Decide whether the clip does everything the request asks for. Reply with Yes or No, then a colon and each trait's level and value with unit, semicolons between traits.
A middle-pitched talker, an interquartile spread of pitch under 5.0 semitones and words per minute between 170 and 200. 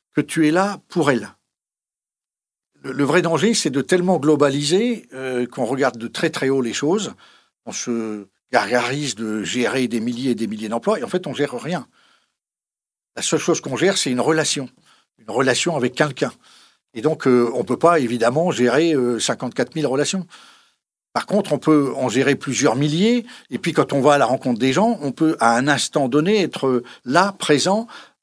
No: medium, 145 Hz; wide, 5.6 semitones; average, 195 wpm